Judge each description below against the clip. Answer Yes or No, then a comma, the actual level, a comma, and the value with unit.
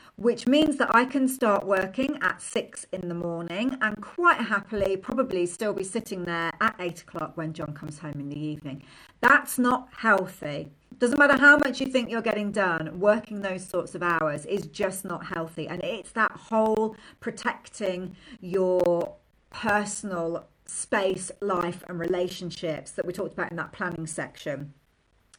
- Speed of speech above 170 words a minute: No, average, 165 wpm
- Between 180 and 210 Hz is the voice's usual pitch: Yes, high, 190 Hz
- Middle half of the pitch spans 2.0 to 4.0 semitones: No, average, 4.8 semitones